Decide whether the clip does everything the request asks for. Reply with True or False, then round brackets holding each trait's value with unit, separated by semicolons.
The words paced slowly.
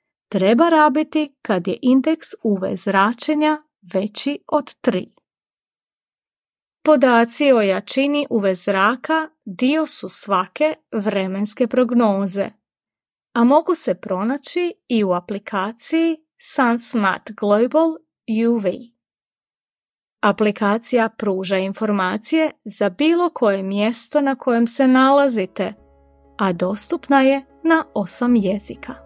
True (95 wpm)